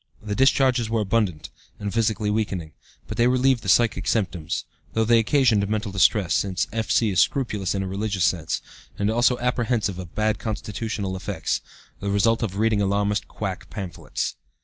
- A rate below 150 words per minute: No, average, 165 wpm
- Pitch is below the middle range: Yes, low, 105 Hz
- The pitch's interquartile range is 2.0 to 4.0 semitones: Yes, average, 2.9 semitones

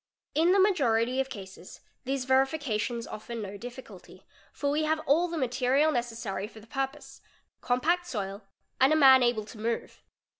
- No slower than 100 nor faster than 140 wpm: No, average, 175 wpm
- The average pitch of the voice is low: No, very high, 255 Hz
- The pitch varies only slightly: No, average, 4.3 semitones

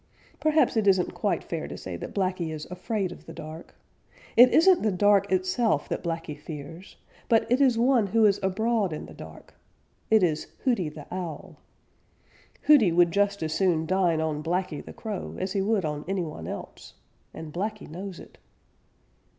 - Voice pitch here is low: No, medium, 185 Hz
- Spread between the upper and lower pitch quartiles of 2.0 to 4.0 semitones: No, average, 4.7 semitones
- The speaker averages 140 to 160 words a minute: No, average, 180 wpm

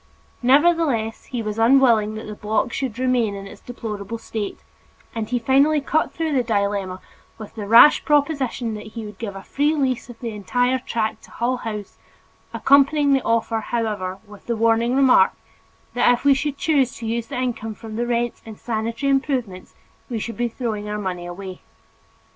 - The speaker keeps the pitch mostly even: No, average, 3.5 semitones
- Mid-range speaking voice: No, high, 230 Hz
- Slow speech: No, average, 185 wpm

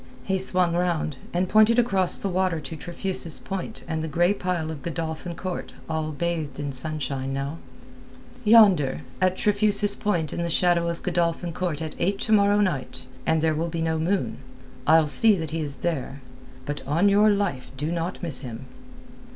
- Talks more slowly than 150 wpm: No, average, 180 wpm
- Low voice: No, medium, 170 Hz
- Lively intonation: No, average, 3.4 semitones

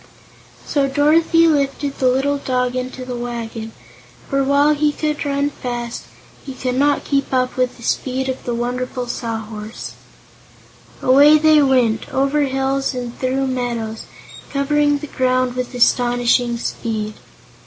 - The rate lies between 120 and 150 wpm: Yes, average, 140 wpm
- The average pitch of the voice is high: Yes, very high, 255 Hz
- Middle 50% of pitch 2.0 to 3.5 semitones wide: Yes, narrow, 2.6 semitones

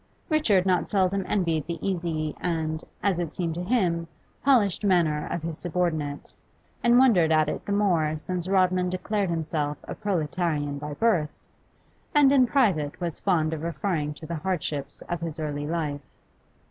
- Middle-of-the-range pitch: Yes, medium, 170 Hz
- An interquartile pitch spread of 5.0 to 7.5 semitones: No, average, 3.5 semitones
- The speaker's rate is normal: Yes, average, 160 wpm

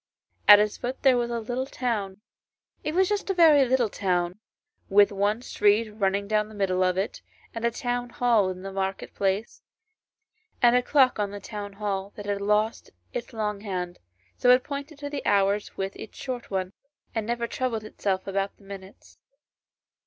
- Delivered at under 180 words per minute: No, average, 185 wpm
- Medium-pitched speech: No, high, 210 Hz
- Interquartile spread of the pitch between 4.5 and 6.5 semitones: No, average, 3.8 semitones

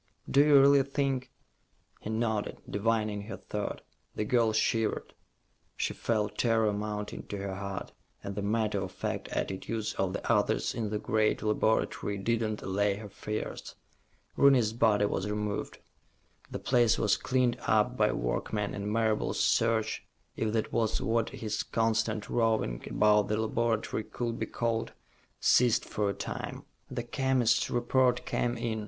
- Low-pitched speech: Yes, low, 110 Hz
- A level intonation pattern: Yes, narrow, 2.0 semitones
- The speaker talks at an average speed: Yes, average, 155 wpm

